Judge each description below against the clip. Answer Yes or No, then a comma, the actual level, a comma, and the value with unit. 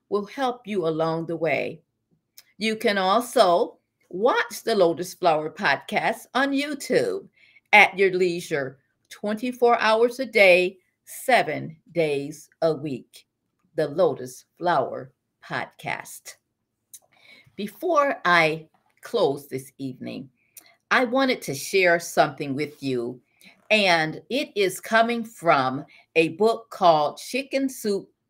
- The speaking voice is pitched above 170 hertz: Yes, medium, 185 Hz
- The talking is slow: Yes, slow, 110 wpm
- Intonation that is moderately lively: No, wide, 7.0 semitones